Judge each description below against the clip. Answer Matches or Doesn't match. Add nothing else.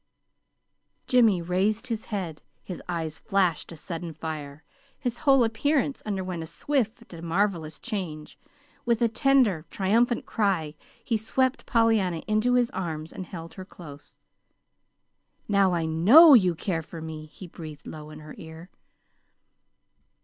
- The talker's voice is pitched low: Doesn't match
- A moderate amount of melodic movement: Doesn't match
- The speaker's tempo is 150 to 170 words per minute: Doesn't match